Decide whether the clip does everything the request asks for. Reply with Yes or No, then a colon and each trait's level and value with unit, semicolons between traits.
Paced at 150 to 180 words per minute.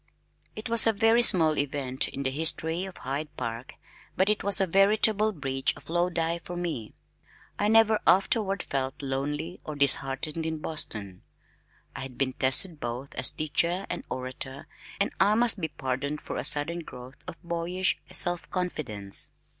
Yes: average, 160 wpm